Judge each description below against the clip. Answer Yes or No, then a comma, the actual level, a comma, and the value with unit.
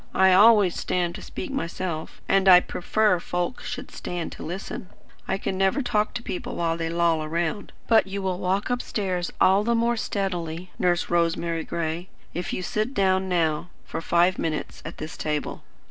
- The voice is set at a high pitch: No, medium, 180 Hz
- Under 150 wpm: No, average, 175 wpm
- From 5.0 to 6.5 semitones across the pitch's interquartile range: No, average, 2.8 semitones